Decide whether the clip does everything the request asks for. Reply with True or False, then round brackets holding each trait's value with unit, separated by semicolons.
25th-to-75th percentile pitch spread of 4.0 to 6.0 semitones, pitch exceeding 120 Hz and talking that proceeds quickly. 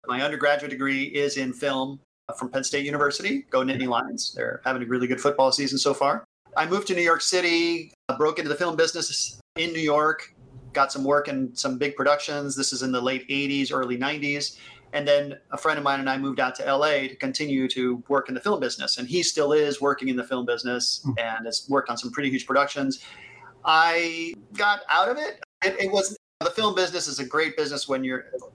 False (3.0 semitones; 140 Hz; 220 wpm)